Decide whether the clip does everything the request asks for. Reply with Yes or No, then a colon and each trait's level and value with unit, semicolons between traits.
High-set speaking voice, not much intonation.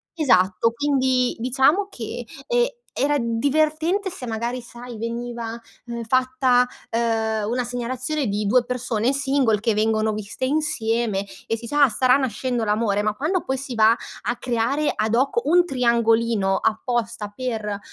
No: high, 240 Hz; average, 3.1 semitones